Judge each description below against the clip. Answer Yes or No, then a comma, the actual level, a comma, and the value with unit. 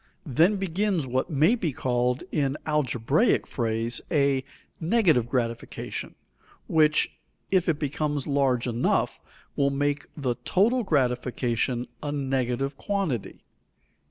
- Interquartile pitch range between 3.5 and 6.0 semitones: Yes, average, 4.3 semitones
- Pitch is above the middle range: No, medium, 140 Hz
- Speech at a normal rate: No, slow, 110 wpm